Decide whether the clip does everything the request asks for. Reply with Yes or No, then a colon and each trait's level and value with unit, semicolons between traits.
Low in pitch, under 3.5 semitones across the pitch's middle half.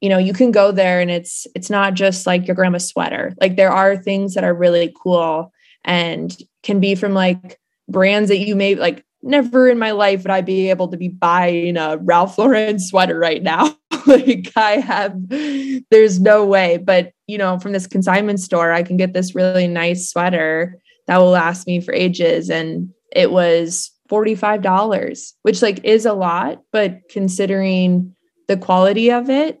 No: high, 190 Hz; average, 2.7 semitones